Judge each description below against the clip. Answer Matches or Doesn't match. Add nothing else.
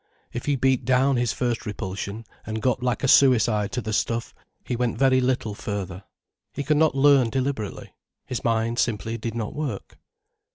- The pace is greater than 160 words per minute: Matches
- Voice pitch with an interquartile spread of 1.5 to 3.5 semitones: Matches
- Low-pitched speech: Matches